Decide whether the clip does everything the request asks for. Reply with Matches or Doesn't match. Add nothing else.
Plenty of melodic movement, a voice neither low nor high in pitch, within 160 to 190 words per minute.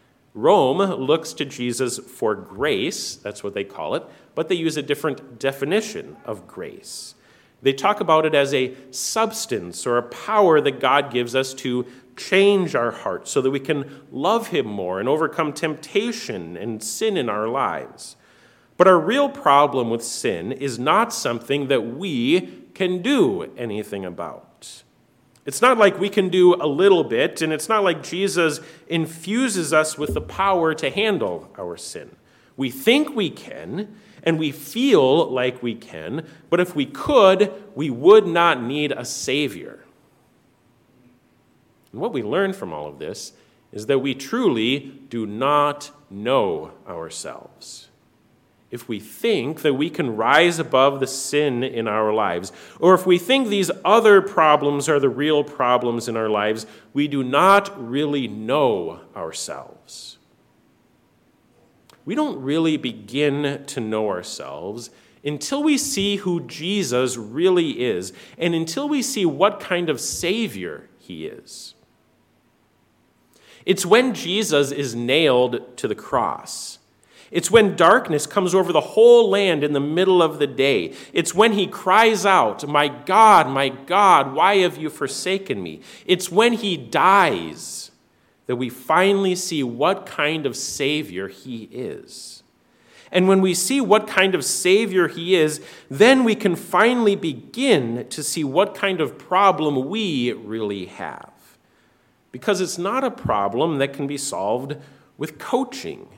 Doesn't match